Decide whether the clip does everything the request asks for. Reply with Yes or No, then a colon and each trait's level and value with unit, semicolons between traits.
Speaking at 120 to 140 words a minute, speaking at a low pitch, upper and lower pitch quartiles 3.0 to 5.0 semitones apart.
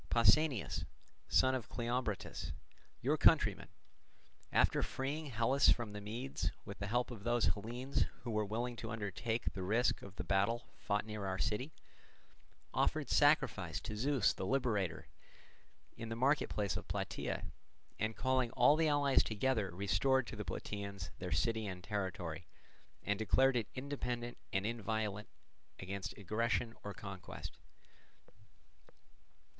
Yes: slow, 135 wpm; low, 110 Hz; average, 3.7 semitones